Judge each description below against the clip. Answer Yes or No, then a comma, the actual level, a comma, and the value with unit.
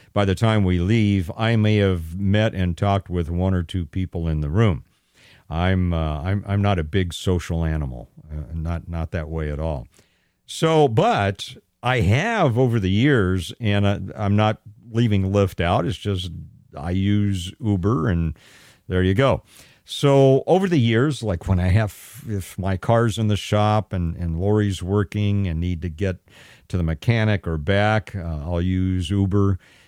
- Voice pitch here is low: Yes, low, 100 Hz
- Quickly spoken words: No, average, 180 wpm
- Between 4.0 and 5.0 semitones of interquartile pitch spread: No, average, 3.4 semitones